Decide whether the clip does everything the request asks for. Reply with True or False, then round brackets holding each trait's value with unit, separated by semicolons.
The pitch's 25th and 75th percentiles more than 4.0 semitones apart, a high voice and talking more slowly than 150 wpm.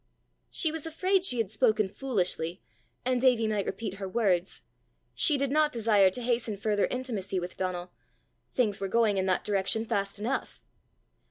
False (4.6 semitones; 215 Hz; 165 wpm)